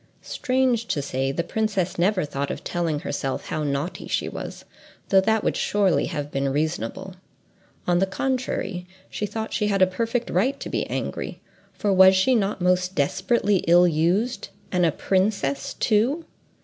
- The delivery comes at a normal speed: Yes, average, 165 wpm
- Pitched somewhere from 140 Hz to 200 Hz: Yes, medium, 185 Hz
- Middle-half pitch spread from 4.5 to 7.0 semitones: Yes, average, 4.9 semitones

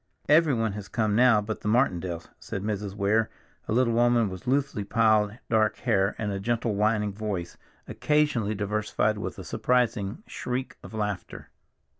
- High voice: No, low, 110 Hz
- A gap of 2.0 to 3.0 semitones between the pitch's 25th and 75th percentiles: Yes, average, 2.7 semitones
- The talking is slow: No, average, 155 wpm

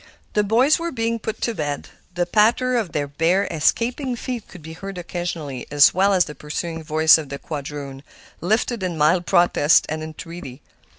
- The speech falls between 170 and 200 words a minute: Yes, average, 180 wpm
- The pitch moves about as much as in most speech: No, wide, 6.2 semitones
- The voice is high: No, medium, 175 Hz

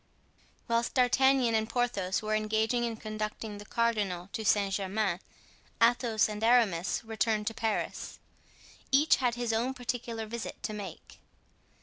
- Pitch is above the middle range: Yes, high, 220 Hz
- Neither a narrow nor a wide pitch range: No, narrow, 2.2 semitones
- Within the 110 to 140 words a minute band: Yes, slow, 135 wpm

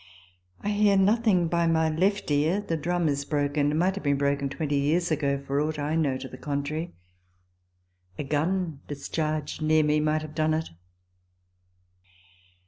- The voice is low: No, medium, 155 Hz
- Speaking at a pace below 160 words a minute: No, average, 165 wpm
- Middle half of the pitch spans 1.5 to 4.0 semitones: Yes, average, 2.9 semitones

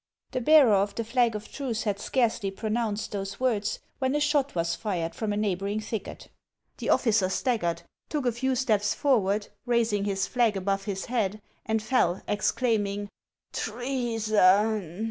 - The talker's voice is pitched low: No, high, 215 Hz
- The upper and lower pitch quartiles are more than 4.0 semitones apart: No, average, 3.3 semitones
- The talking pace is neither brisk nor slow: Yes, average, 160 wpm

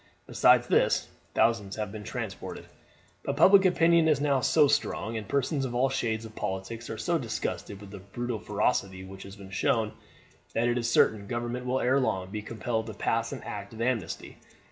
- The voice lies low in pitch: Yes, low, 115 Hz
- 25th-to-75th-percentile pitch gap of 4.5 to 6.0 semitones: No, average, 3.6 semitones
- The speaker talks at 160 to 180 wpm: No, average, 190 wpm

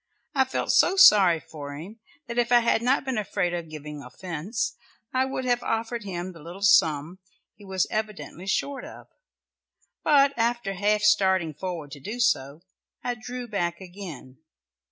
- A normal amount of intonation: No, wide, 5.9 semitones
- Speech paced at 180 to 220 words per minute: No, average, 165 wpm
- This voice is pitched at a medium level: No, high, 195 Hz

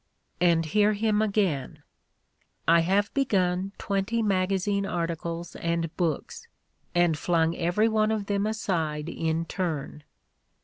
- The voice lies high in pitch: No, medium, 180 Hz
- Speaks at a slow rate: Yes, slow, 130 wpm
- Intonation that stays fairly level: No, average, 3.6 semitones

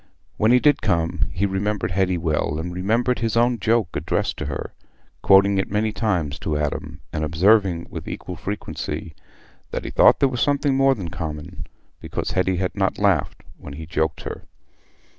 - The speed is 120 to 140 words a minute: No, average, 180 wpm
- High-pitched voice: No, very low, 95 Hz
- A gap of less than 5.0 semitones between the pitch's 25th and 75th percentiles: No, average, 5.3 semitones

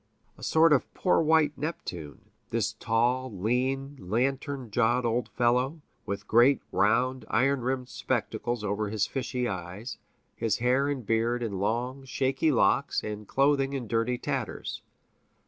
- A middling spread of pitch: Yes, average, 3.4 semitones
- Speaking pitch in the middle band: No, low, 125 Hz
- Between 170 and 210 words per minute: No, average, 140 wpm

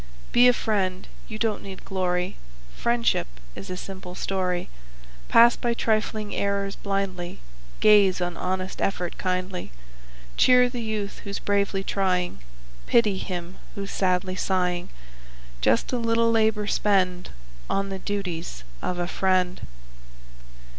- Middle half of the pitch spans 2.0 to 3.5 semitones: Yes, average, 2.7 semitones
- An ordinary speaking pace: No, slow, 125 wpm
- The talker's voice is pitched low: No, high, 195 Hz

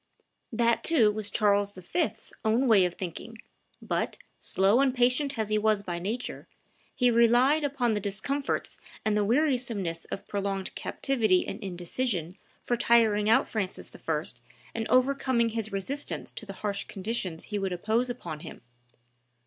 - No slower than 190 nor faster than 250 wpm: No, average, 150 wpm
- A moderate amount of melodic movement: Yes, average, 3.8 semitones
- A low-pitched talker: No, high, 220 Hz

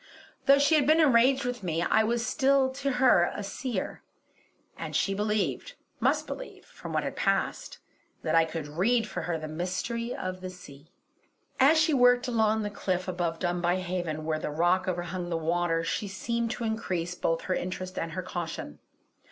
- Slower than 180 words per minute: No, average, 185 wpm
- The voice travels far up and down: Yes, wide, 5.7 semitones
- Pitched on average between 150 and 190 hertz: Yes, medium, 185 Hz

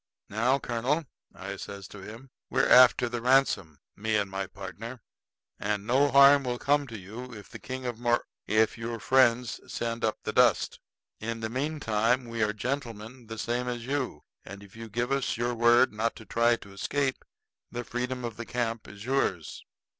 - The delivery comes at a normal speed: Yes, average, 185 wpm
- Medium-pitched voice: No, low, 115 Hz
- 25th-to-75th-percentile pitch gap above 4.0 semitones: No, average, 2.8 semitones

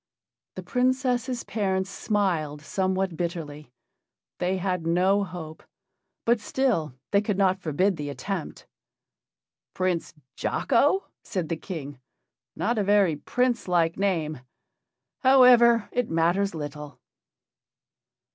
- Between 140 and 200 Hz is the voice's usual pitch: Yes, high, 190 Hz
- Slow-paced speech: Yes, slow, 110 wpm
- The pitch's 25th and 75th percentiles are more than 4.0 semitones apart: Yes, average, 4.9 semitones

